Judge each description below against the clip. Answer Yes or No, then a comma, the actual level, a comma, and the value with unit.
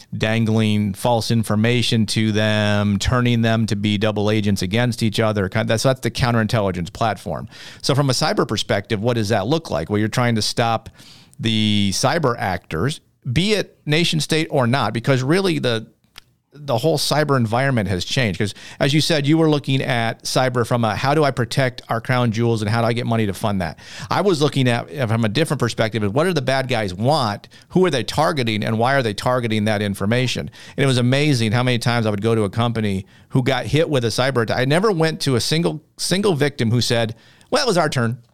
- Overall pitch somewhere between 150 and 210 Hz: No, low, 120 Hz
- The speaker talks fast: Yes, fast, 220 wpm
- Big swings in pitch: No, average, 3.8 semitones